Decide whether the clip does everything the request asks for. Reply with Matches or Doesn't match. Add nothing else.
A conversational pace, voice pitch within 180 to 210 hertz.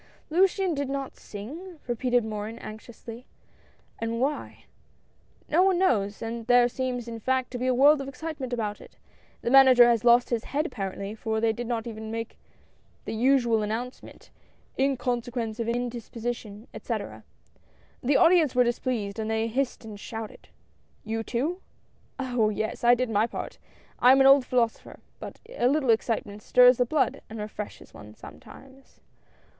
Doesn't match